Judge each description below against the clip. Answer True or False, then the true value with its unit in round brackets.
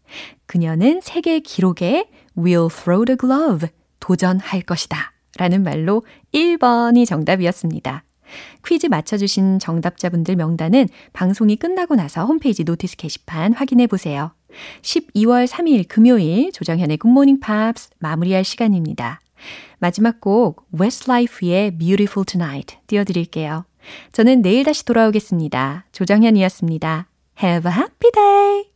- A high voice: True (195 Hz)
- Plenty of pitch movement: True (6.1 semitones)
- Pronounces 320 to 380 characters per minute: True (365 characters per minute)